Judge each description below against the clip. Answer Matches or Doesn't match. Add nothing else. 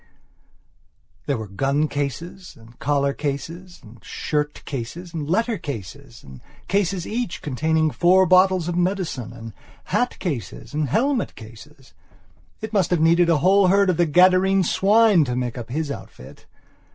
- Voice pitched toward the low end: Doesn't match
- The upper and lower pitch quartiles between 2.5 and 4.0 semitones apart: Doesn't match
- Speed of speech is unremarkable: Matches